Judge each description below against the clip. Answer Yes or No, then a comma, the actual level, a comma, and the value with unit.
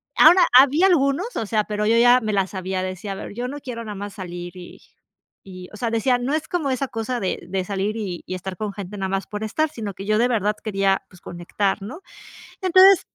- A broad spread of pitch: No, average, 4.7 semitones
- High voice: Yes, high, 215 Hz